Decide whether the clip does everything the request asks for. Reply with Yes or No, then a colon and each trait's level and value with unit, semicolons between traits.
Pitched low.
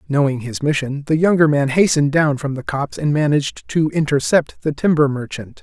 No: medium, 145 Hz